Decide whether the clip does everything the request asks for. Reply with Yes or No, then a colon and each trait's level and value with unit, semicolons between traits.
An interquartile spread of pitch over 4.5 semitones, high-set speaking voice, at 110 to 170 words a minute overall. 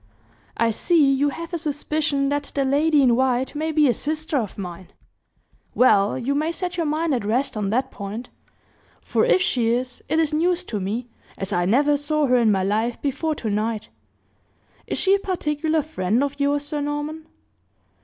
No: average, 5.0 semitones; very high, 280 Hz; average, 185 wpm